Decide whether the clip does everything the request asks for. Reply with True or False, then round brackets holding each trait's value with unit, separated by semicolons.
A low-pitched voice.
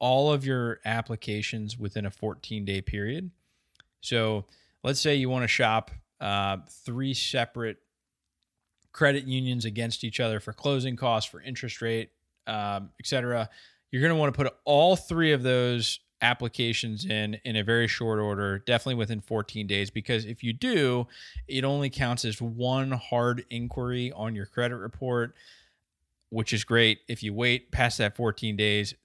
True (115 Hz)